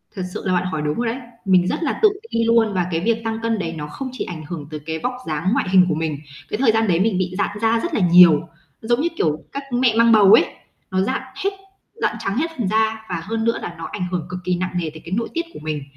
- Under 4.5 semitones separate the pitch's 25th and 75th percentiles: No, average, 5.2 semitones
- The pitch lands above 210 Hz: No, high, 190 Hz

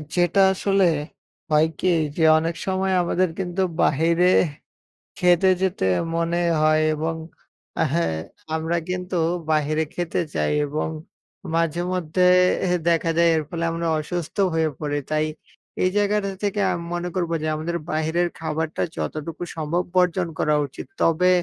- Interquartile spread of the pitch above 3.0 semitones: No, narrow, 2.4 semitones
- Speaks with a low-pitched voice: No, medium, 170 Hz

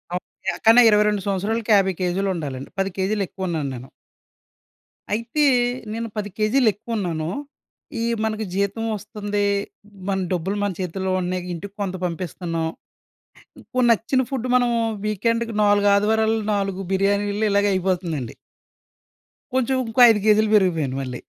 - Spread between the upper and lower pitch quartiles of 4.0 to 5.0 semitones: No, average, 3.1 semitones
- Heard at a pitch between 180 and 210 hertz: Yes, high, 200 Hz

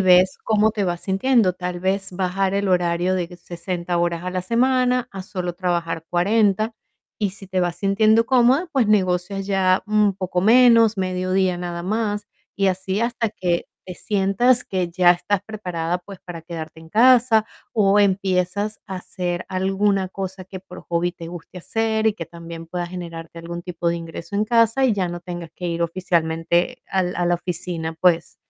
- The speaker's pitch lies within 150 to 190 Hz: Yes, medium, 185 Hz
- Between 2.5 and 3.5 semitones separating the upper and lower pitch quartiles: Yes, average, 2.9 semitones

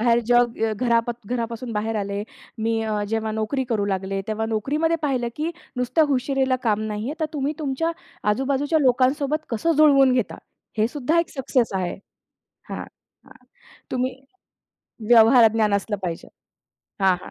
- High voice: Yes, high, 240 Hz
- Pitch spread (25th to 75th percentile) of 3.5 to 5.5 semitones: Yes, average, 3.9 semitones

